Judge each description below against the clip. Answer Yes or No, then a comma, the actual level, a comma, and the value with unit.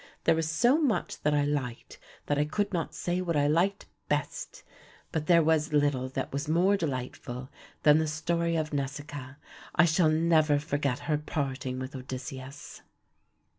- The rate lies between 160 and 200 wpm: Yes, average, 165 wpm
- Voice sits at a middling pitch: Yes, medium, 150 Hz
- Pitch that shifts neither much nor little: Yes, average, 3.0 semitones